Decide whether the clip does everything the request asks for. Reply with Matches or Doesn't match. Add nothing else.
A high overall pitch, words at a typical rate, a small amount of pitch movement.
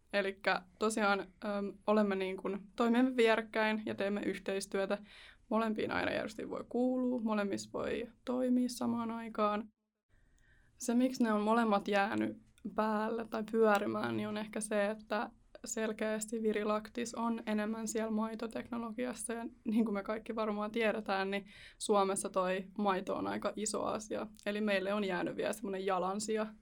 Matches